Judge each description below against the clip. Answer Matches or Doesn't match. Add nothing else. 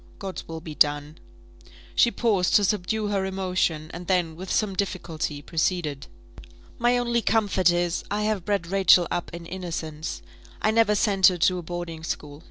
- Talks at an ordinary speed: Matches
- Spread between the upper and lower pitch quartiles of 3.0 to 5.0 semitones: Matches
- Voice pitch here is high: Doesn't match